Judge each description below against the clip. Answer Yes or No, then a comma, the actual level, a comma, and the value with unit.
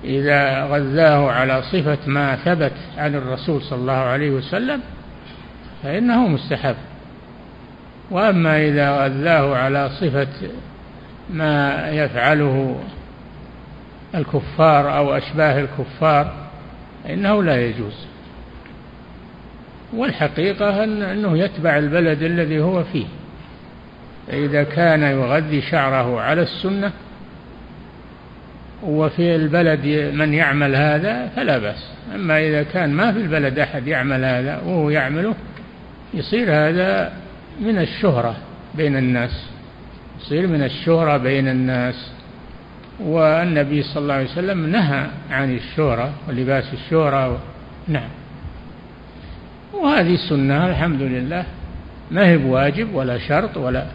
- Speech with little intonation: No, average, 3.7 semitones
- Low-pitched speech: No, medium, 150 Hz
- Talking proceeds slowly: No, average, 100 wpm